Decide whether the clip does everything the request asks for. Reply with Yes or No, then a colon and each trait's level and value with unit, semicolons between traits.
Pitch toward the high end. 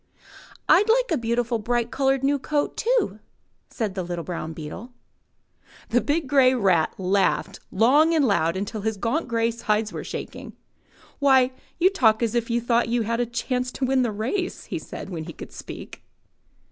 Yes: high, 235 Hz